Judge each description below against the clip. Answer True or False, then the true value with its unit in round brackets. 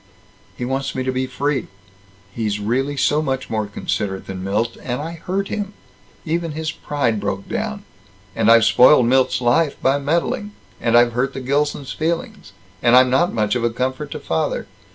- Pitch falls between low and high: False (130 Hz)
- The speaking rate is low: False (180 wpm)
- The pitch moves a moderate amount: True (4.5 semitones)